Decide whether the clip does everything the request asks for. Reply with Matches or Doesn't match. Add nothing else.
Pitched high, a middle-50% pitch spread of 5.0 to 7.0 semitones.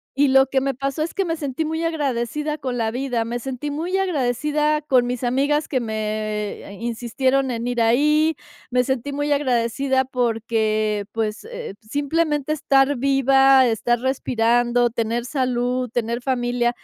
Doesn't match